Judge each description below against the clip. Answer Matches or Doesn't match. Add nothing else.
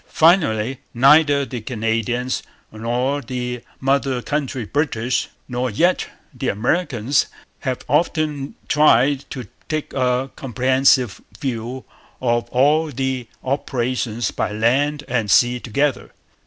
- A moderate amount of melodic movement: Matches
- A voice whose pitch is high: Doesn't match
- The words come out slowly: Matches